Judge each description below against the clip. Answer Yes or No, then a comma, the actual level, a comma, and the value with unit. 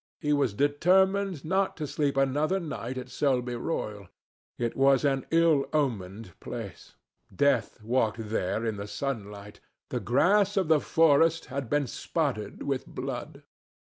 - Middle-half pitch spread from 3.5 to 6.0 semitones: Yes, wide, 5.5 semitones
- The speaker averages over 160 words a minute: No, average, 140 wpm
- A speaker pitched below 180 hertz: Yes, medium, 140 Hz